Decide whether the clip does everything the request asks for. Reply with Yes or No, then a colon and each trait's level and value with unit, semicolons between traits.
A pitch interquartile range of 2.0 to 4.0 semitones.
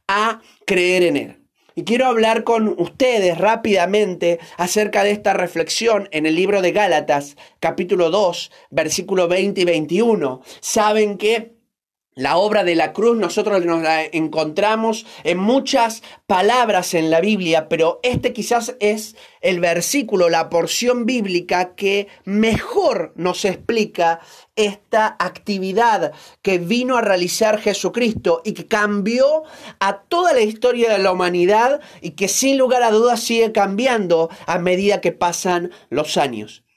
No: average, 4.4 semitones